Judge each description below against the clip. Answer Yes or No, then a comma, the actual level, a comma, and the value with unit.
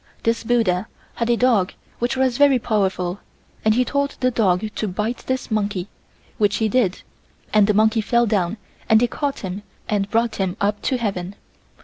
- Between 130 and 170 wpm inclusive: No, average, 185 wpm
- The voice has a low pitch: No, high, 220 Hz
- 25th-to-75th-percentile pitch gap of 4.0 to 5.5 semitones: No, average, 3.2 semitones